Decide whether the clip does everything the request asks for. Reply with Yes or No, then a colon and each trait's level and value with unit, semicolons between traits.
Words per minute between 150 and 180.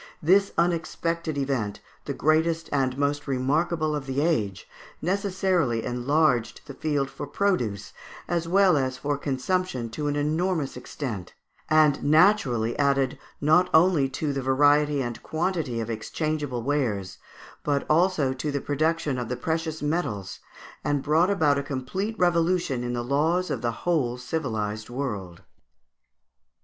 No: average, 140 wpm